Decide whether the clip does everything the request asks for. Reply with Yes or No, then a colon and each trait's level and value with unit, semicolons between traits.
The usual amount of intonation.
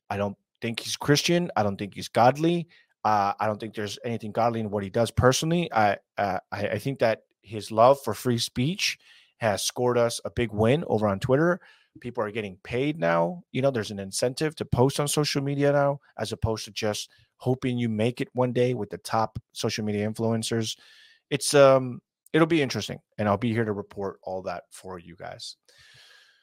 Yes: average, 4.5 semitones